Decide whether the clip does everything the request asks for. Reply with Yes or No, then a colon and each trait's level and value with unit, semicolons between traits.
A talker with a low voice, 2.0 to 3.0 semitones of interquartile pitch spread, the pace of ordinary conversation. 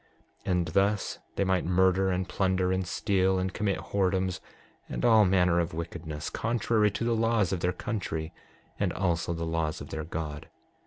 Yes: very low, 95 Hz; average, 2.7 semitones; average, 175 wpm